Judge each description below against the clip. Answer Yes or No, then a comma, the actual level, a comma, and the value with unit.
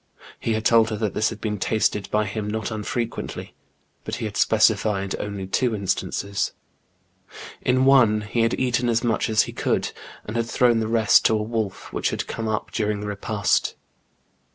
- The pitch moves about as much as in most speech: No, narrow, 1.8 semitones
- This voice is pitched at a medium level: No, low, 110 Hz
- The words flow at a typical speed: Yes, average, 185 wpm